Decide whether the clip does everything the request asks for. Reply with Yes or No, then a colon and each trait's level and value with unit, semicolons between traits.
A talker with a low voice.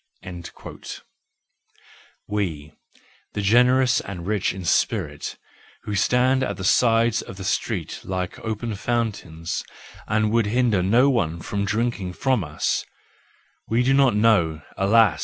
Yes: low, 105 Hz